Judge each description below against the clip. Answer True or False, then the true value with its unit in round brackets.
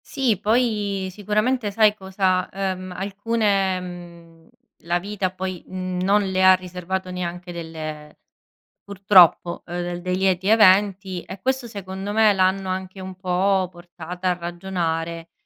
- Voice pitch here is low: False (185 Hz)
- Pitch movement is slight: True (2.1 semitones)